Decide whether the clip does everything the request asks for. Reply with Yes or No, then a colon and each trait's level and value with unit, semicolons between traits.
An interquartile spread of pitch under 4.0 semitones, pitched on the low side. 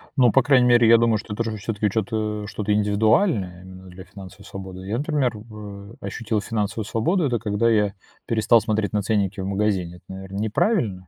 Yes: narrow, 2.5 semitones; low, 105 Hz